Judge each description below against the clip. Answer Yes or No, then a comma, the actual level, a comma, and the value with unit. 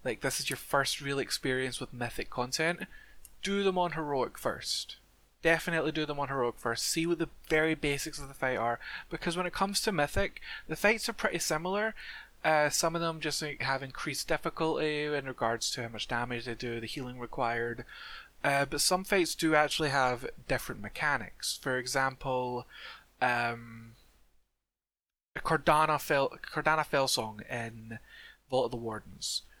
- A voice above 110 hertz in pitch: Yes, medium, 140 Hz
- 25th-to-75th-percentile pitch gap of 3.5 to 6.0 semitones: Yes, average, 5.1 semitones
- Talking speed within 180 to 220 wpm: No, average, 165 wpm